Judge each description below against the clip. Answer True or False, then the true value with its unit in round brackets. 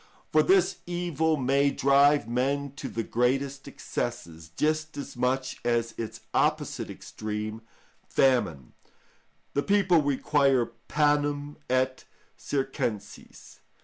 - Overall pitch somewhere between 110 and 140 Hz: True (135 Hz)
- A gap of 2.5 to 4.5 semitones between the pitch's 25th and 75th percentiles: True (3.3 semitones)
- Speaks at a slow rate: True (105 wpm)